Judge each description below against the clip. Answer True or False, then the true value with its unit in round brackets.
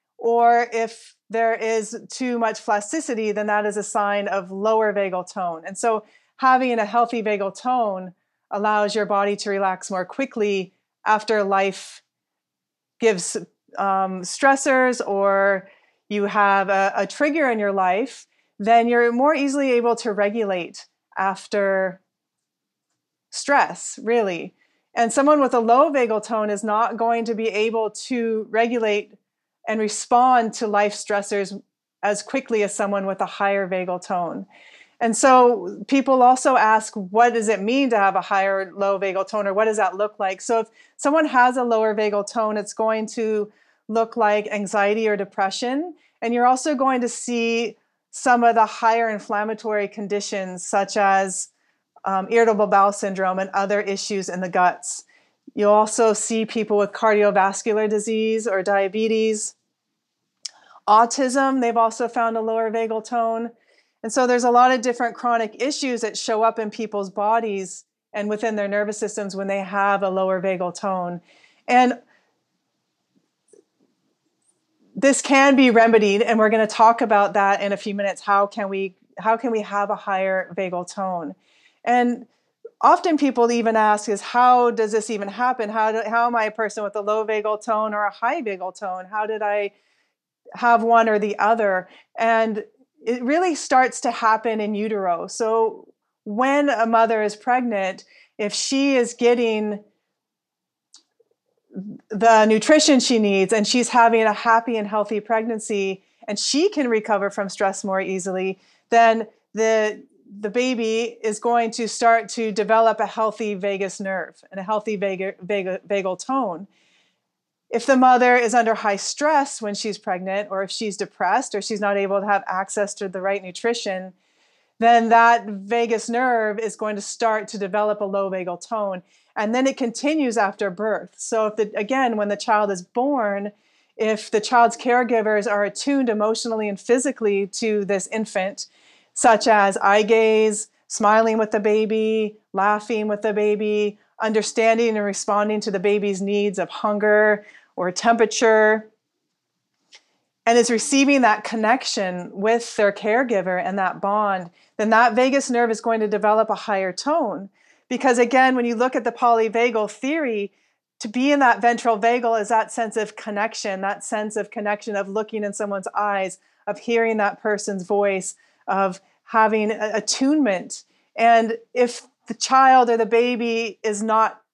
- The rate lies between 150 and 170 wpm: True (160 wpm)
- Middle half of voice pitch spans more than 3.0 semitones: False (2.4 semitones)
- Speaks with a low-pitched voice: False (220 Hz)